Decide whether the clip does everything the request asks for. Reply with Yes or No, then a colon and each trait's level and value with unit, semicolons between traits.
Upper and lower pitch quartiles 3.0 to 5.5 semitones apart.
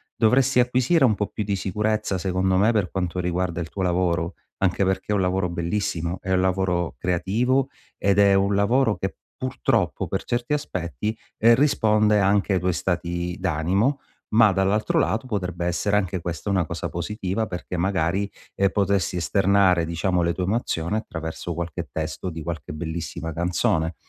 Yes: average, 3.3 semitones